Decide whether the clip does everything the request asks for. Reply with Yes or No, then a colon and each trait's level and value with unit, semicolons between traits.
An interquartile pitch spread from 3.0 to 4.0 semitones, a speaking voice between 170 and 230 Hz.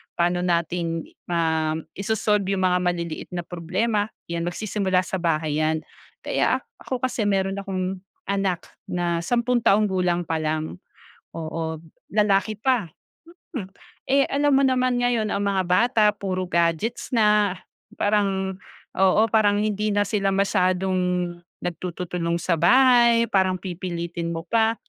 Yes: average, 3.6 semitones; high, 190 Hz